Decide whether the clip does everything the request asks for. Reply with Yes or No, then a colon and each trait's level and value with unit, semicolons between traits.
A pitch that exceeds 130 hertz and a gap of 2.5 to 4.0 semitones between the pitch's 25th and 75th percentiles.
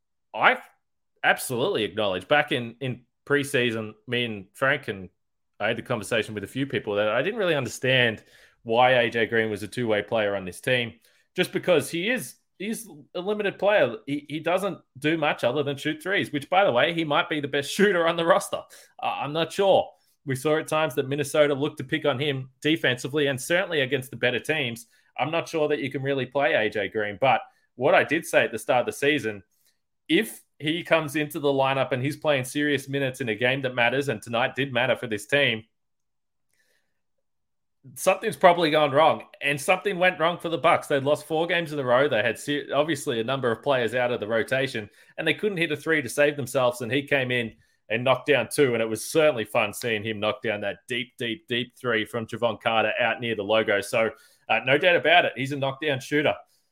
No: medium, 140 Hz; average, 4.5 semitones